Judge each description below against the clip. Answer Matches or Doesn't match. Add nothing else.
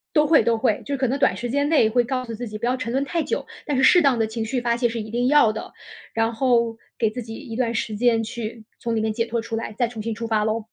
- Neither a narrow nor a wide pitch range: Doesn't match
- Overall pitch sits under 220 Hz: Doesn't match